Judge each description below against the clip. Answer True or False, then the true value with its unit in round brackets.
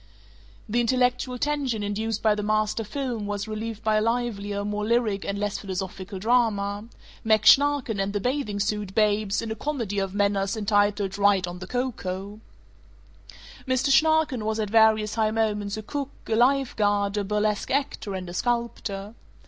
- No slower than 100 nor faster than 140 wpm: False (165 wpm)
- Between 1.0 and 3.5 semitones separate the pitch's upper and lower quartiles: True (2.7 semitones)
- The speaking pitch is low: False (215 Hz)